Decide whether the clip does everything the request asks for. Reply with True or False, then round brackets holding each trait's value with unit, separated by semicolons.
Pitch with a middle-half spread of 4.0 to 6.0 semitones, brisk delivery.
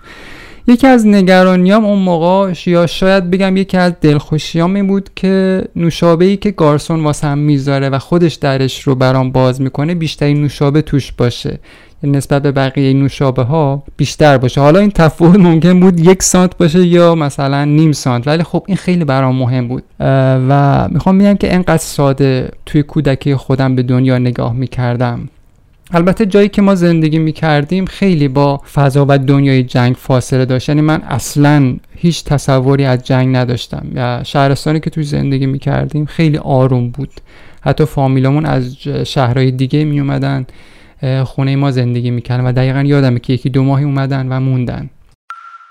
True (4.3 semitones; 165 wpm)